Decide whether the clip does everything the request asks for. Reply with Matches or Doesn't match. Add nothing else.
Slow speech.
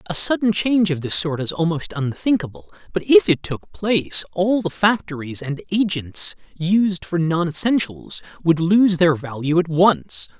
Doesn't match